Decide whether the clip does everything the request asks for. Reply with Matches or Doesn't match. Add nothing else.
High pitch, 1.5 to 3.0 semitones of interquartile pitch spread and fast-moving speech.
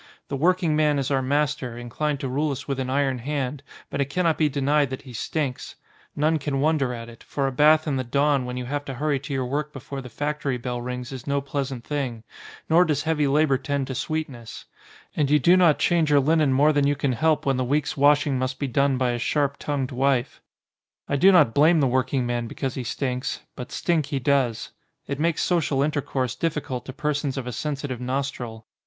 Doesn't match